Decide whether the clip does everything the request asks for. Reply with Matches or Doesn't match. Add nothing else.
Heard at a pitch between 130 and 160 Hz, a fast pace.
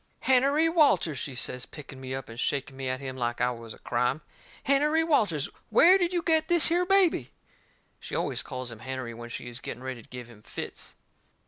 Matches